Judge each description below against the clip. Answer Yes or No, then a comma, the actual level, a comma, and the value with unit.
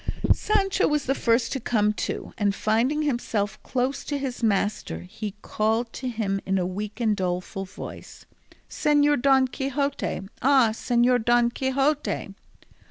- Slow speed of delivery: No, average, 145 wpm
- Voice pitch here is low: No, high, 240 Hz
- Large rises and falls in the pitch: No, average, 4.4 semitones